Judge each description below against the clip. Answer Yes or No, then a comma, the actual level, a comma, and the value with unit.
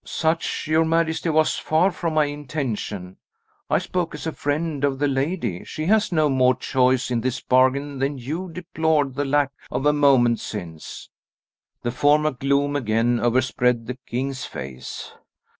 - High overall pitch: No, medium, 140 Hz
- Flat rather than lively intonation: No, average, 3.6 semitones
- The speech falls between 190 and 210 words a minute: No, average, 160 wpm